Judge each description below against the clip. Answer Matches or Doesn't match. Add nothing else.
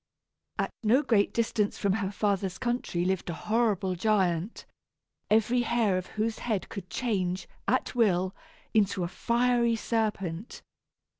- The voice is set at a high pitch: Matches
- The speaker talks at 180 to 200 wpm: Doesn't match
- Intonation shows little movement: Doesn't match